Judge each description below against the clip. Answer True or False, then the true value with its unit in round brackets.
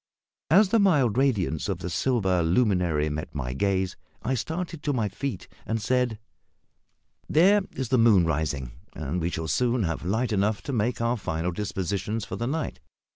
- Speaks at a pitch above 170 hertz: False (105 Hz)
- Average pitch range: False (6.5 semitones)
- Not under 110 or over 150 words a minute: False (175 wpm)